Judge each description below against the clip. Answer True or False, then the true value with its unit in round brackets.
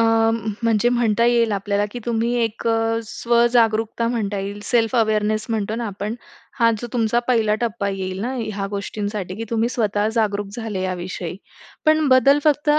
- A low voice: False (225 Hz)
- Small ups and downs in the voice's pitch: True (2.3 semitones)